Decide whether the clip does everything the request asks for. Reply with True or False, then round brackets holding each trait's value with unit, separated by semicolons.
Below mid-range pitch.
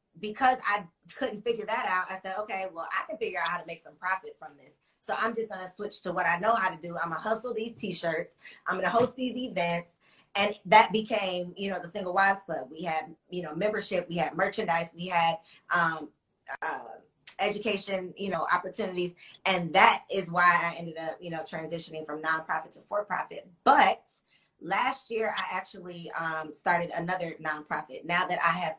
False (180 Hz)